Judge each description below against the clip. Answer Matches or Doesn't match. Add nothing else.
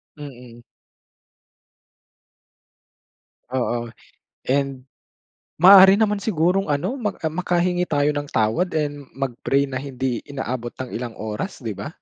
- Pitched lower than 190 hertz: Matches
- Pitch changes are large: Matches